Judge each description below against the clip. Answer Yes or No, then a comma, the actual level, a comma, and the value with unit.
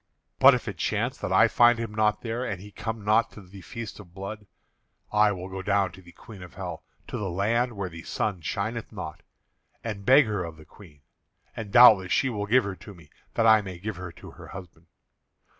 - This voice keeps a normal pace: No, fast, 225 wpm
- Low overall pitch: Yes, low, 100 Hz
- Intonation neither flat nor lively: Yes, average, 3.2 semitones